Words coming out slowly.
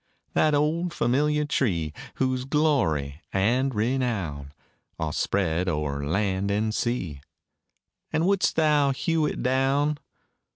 Yes: slow, 115 wpm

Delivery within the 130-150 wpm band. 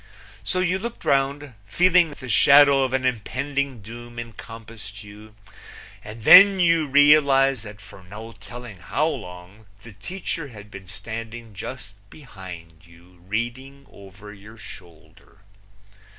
Yes: slow, 135 wpm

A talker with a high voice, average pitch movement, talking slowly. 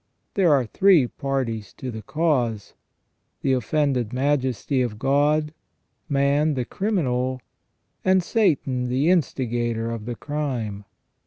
No: low, 130 Hz; average, 3.9 semitones; slow, 120 wpm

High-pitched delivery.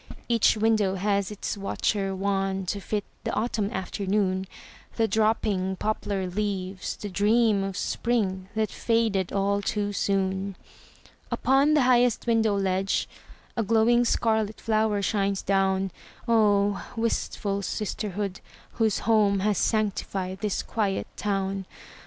Yes: high, 205 Hz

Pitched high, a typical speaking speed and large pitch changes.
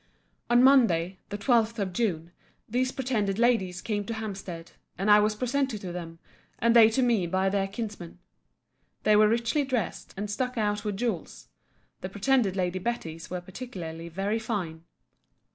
No: high, 210 Hz; average, 160 wpm; average, 4.3 semitones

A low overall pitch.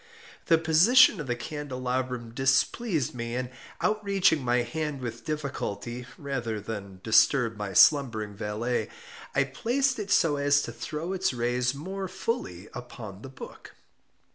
Yes: low, 130 Hz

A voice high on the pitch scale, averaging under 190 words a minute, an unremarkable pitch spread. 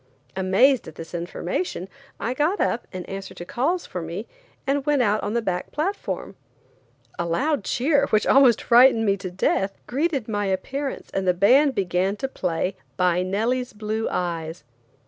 No: high, 210 Hz; average, 165 wpm; wide, 6.4 semitones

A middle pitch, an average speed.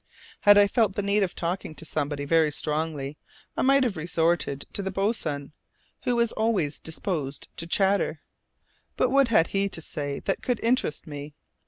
Yes: medium, 170 Hz; average, 175 wpm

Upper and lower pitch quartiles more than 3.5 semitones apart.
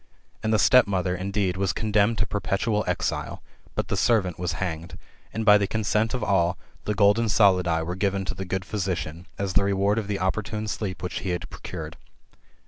No: narrow, 2.6 semitones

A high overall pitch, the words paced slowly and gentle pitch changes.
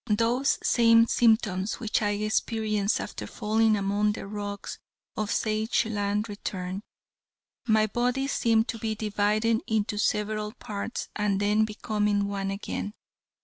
Yes: high, 215 Hz; slow, 125 wpm; narrow, 1.5 semitones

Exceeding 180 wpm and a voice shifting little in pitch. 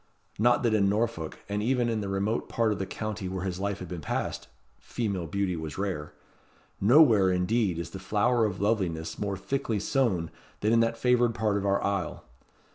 No: average, 195 wpm; average, 3.5 semitones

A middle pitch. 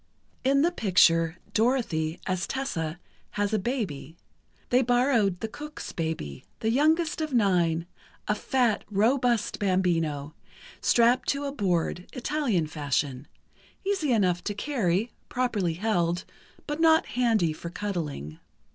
No: high, 205 Hz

